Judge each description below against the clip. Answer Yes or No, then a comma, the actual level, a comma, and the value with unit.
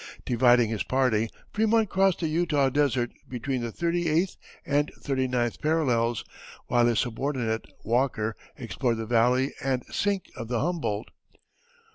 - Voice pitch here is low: Yes, low, 130 Hz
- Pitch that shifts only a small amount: No, average, 4.7 semitones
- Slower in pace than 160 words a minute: Yes, average, 140 wpm